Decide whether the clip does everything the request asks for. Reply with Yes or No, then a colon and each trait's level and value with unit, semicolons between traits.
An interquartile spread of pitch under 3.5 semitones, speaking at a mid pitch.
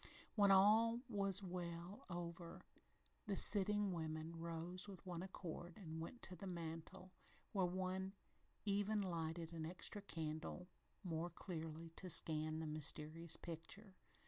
Yes: average, 2.9 semitones; medium, 175 Hz